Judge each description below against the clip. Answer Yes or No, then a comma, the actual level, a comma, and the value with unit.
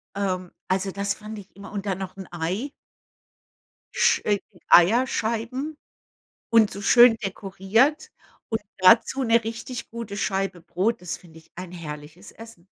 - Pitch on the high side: Yes, high, 200 Hz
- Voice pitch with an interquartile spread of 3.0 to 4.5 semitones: Yes, average, 3.7 semitones